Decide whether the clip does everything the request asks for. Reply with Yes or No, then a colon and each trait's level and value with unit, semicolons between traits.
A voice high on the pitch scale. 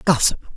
No: medium, 150 Hz